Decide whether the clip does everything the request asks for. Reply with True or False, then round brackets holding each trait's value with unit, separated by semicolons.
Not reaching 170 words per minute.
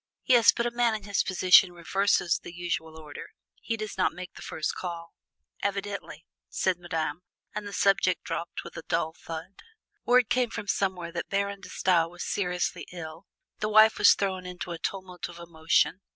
False (180 wpm)